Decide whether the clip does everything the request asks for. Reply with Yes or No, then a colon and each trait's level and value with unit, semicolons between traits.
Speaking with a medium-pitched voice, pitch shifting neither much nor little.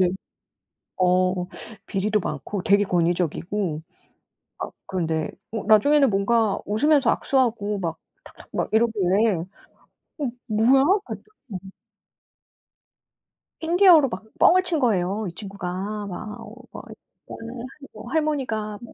No: high, 210 Hz; average, 4.1 semitones